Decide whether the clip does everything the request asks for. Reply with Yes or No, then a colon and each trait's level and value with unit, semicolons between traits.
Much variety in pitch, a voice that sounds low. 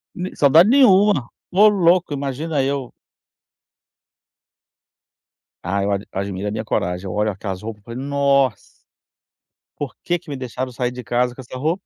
Yes: wide, 6.7 semitones; low, 130 Hz